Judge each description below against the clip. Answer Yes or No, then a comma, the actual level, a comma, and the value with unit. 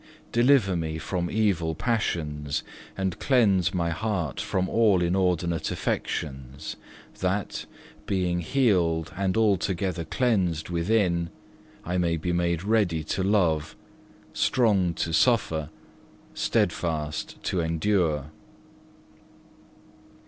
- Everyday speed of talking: No, slow, 100 wpm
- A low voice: Yes, very low, 85 Hz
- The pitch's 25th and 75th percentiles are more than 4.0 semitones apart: No, average, 3.5 semitones